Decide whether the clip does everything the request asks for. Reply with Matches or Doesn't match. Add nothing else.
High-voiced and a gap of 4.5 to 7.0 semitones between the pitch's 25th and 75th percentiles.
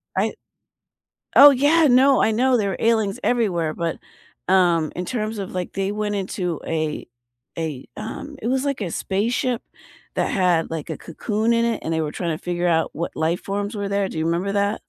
Matches